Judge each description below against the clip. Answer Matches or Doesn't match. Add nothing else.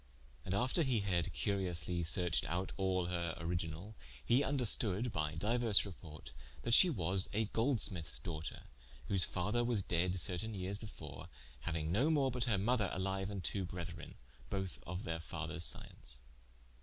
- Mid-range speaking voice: Doesn't match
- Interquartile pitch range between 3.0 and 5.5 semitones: Matches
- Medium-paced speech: Matches